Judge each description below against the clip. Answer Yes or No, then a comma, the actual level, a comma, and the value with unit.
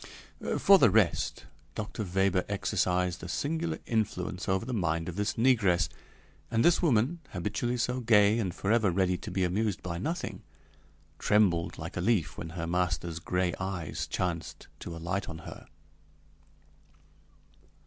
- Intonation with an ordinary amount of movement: Yes, average, 4.3 semitones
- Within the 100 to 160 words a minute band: Yes, average, 145 wpm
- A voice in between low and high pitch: No, very low, 95 Hz